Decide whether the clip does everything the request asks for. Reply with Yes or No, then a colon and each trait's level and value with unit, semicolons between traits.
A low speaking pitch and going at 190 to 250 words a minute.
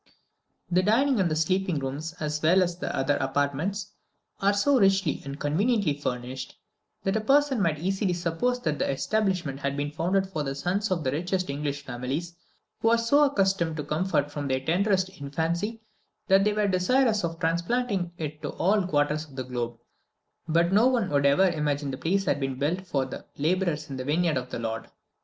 No: medium, 170 Hz; average, 195 wpm